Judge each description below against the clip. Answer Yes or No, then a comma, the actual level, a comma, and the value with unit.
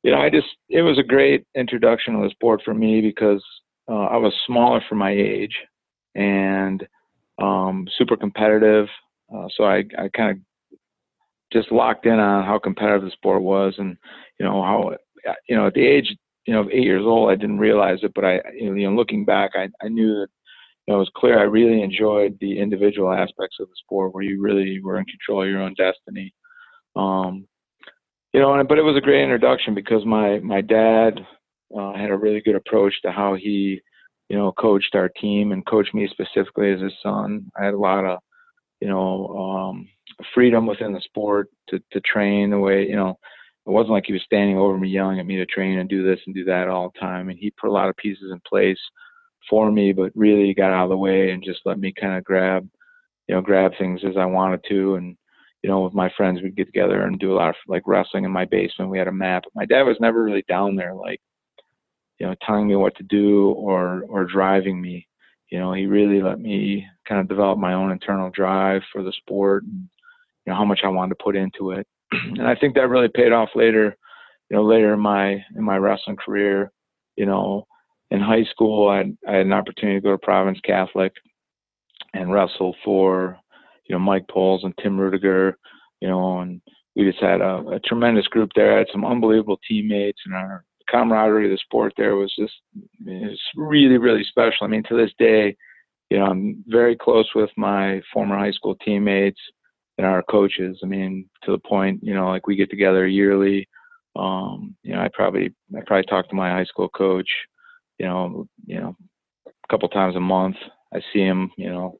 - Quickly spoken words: Yes, fast, 215 wpm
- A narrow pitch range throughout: Yes, narrow, 2.3 semitones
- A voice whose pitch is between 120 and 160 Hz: No, low, 100 Hz